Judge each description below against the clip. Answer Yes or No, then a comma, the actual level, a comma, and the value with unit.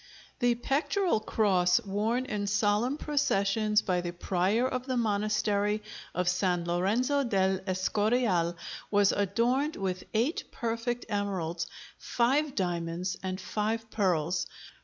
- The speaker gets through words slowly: Yes, slow, 115 wpm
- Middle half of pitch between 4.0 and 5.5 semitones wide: Yes, average, 4.3 semitones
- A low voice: No, high, 205 Hz